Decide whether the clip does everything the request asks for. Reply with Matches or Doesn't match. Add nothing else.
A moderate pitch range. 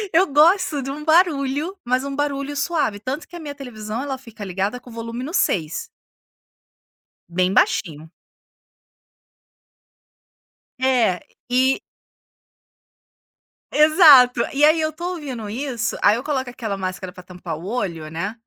Doesn't match